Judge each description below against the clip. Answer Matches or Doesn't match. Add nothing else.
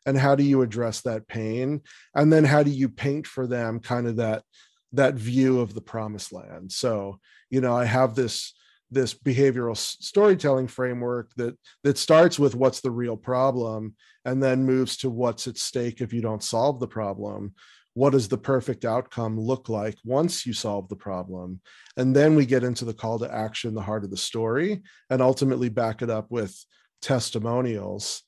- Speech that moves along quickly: Doesn't match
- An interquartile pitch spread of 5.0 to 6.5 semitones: Doesn't match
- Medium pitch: Doesn't match